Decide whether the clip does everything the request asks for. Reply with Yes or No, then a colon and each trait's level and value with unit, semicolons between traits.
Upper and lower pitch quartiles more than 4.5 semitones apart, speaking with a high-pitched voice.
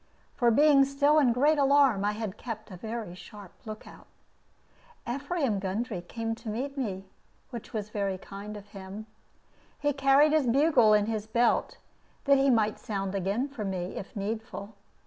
Yes: average, 5.1 semitones; high, 225 Hz